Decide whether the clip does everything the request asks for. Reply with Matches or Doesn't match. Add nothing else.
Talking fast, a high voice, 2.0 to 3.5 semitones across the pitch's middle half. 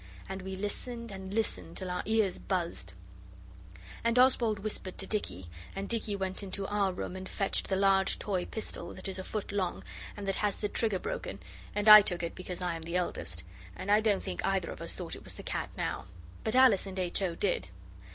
Matches